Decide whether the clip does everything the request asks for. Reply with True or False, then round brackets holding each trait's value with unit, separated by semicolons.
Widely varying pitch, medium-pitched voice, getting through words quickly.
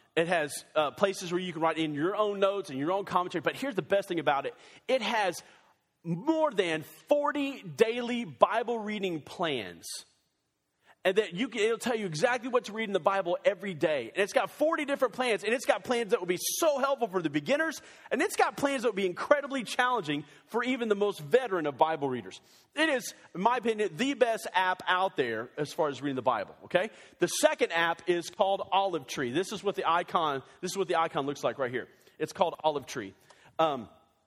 False (6.7 semitones; 195 Hz; 220 wpm)